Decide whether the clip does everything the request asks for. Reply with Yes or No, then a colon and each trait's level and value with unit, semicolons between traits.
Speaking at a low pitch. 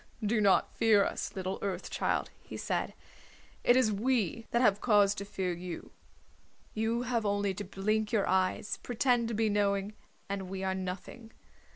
No: high, 205 Hz